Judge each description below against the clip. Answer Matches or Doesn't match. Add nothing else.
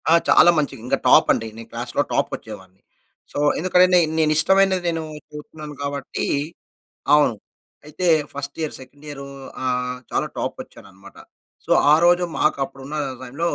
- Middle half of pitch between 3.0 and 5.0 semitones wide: Matches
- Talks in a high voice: Doesn't match